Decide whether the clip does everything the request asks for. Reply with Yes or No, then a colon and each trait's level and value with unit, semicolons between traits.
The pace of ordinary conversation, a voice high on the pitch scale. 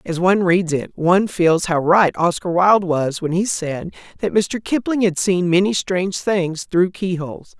No: average, 190 wpm; medium, 180 Hz